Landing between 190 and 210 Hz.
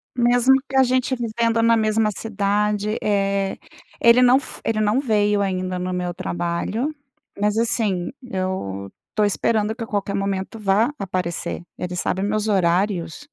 Yes: high, 205 Hz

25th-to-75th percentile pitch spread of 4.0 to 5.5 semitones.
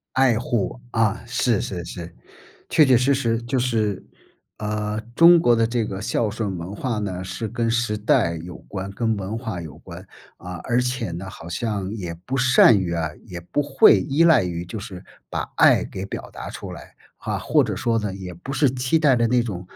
Yes: average, 4.6 semitones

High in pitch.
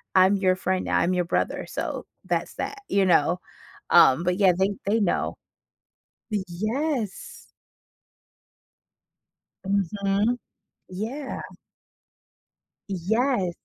Yes: high, 195 Hz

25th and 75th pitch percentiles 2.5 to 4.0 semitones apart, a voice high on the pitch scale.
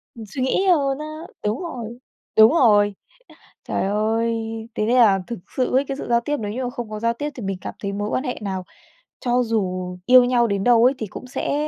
Yes: average, 3.5 semitones; high, 235 Hz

